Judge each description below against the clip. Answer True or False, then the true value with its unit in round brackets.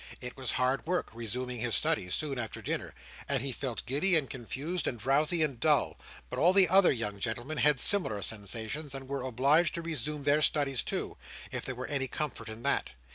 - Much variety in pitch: False (4.1 semitones)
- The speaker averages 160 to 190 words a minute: False (200 wpm)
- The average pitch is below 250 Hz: True (135 Hz)